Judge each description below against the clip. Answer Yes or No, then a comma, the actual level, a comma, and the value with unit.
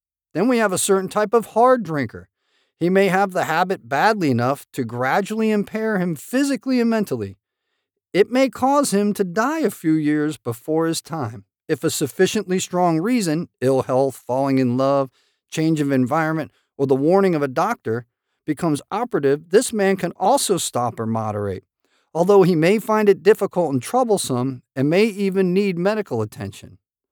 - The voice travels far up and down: Yes, wide, 7.4 semitones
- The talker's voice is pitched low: No, medium, 165 Hz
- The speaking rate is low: No, average, 170 wpm